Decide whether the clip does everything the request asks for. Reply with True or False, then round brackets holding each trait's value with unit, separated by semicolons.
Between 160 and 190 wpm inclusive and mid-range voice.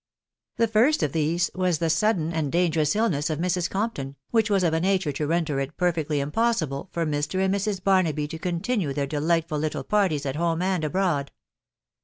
False (200 wpm; 170 Hz)